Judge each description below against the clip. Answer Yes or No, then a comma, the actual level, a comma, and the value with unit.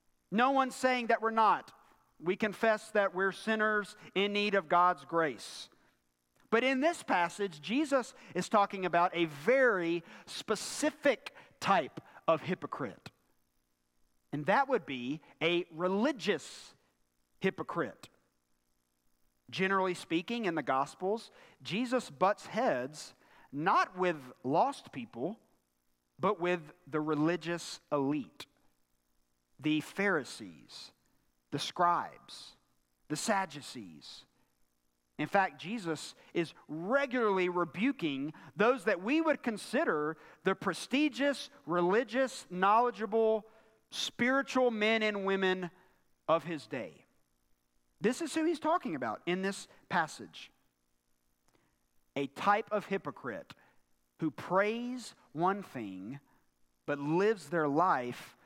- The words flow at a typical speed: No, slow, 105 wpm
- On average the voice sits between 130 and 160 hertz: No, medium, 180 Hz